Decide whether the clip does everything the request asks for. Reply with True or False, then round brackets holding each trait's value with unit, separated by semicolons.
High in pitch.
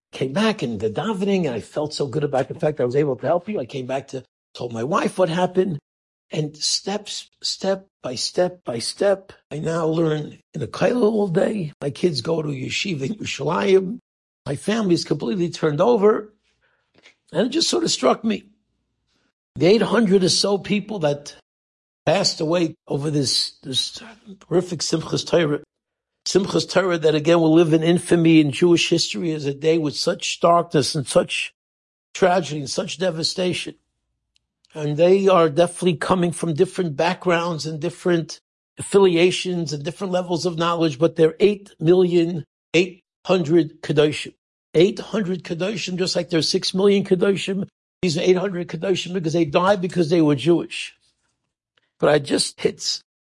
False (175 Hz)